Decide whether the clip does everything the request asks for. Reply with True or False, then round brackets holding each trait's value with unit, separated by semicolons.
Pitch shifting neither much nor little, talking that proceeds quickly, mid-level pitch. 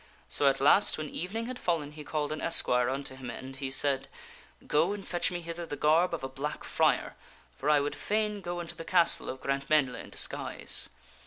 True (4.1 semitones; 215 wpm; 150 Hz)